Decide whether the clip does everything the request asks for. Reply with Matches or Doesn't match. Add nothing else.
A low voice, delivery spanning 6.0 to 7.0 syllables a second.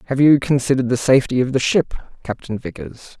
Matches